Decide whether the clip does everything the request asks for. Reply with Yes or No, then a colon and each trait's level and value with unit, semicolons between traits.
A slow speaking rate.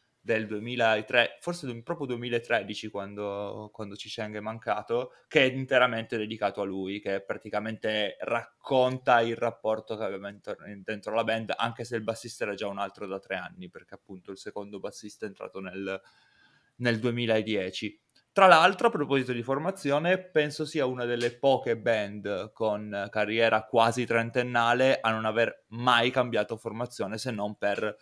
No: average, 160 wpm